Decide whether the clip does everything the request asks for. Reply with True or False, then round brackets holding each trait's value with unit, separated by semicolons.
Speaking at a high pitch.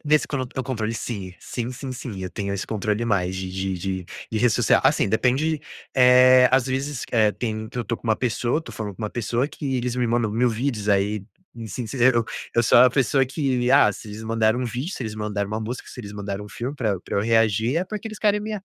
False (115 Hz)